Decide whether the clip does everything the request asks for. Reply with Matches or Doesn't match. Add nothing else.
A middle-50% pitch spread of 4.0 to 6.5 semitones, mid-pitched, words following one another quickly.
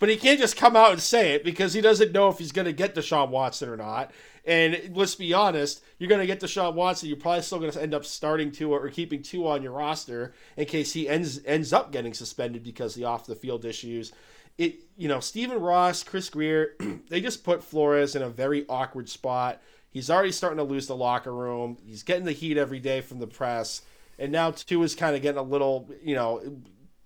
Matches